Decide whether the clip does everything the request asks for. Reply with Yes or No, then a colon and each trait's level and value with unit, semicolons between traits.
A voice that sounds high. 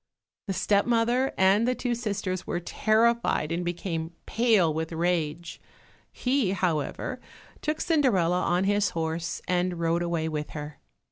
No: medium, 180 Hz